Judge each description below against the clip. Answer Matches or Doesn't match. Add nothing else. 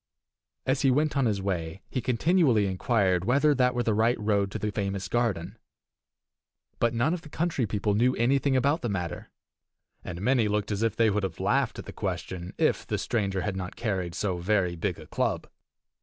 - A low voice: Matches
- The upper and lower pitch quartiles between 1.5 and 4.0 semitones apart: Doesn't match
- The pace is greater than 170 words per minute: Matches